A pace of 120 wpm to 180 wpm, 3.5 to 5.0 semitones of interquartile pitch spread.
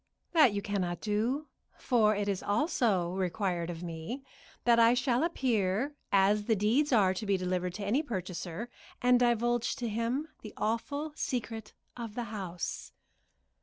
Yes: average, 155 wpm; average, 4.3 semitones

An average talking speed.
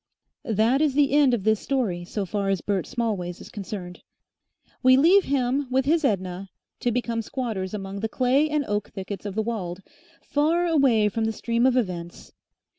Yes: average, 185 wpm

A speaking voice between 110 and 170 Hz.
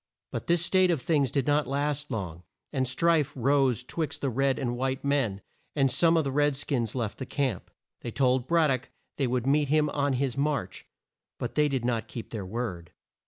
Yes: low, 135 Hz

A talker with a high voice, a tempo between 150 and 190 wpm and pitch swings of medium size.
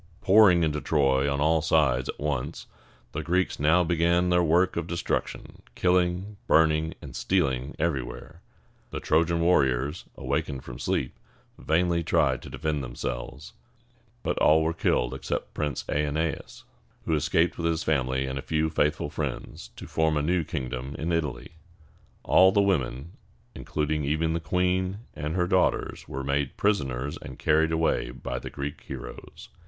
No: very low, 80 Hz; average, 155 wpm; average, 3.4 semitones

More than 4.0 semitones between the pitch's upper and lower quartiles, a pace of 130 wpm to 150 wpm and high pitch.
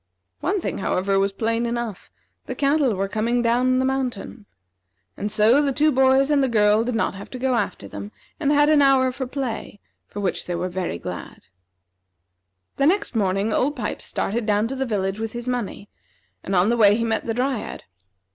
No: average, 4.4 semitones; average, 200 wpm; high, 235 Hz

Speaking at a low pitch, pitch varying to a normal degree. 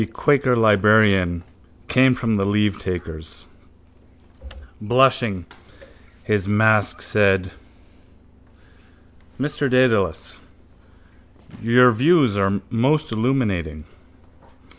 Yes: low, 110 Hz; average, 4.5 semitones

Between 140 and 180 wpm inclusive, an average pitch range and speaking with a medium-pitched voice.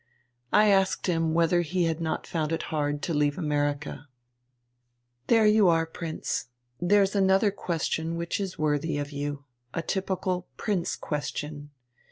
Yes: average, 145 wpm; average, 4.2 semitones; medium, 165 Hz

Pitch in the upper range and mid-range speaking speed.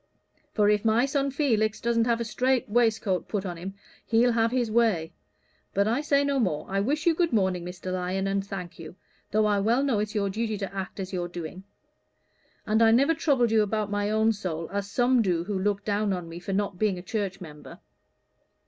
No: high, 210 Hz; fast, 215 wpm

